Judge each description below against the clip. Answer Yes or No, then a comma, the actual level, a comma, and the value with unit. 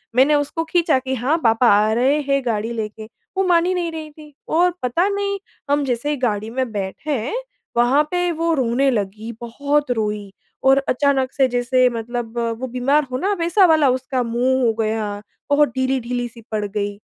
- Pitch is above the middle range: Yes, very high, 255 Hz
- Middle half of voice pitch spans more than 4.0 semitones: Yes, average, 4.4 semitones